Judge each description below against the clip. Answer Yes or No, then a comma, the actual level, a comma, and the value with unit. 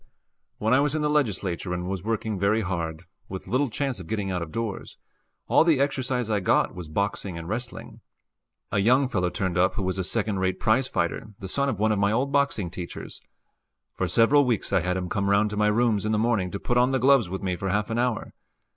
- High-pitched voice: No, low, 105 Hz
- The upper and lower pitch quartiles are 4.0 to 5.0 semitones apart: Yes, average, 4.7 semitones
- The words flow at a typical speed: No, fast, 235 wpm